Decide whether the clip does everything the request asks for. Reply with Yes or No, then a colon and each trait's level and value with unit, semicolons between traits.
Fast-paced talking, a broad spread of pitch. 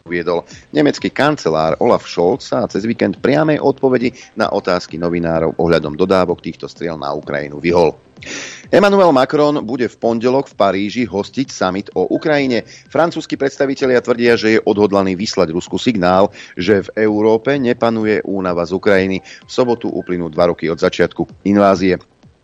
No: average, 145 wpm; wide, 6.3 semitones